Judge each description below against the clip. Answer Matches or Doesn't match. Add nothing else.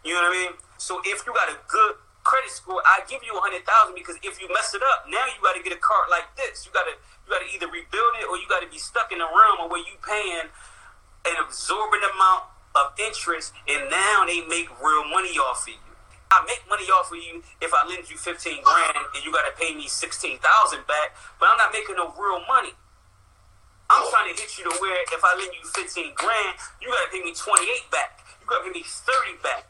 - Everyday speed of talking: Doesn't match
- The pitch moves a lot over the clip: Matches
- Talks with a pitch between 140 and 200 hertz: Matches